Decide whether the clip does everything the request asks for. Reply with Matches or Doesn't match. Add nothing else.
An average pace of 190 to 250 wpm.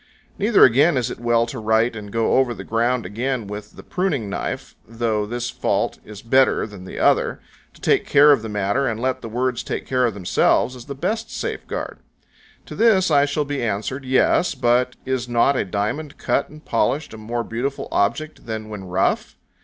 Matches